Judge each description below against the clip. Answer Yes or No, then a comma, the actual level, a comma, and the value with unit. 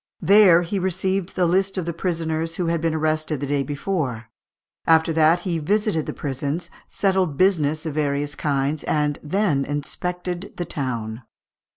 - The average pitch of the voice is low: No, medium, 160 Hz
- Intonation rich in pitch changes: No, average, 3.7 semitones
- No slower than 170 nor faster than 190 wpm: No, average, 160 wpm